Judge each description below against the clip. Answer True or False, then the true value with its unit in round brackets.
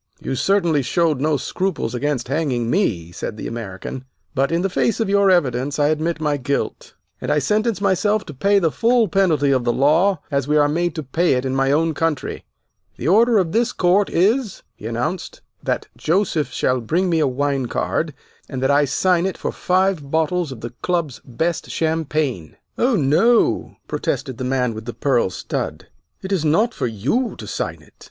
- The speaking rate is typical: True (195 wpm)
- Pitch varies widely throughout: True (5.9 semitones)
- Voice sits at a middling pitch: True (155 Hz)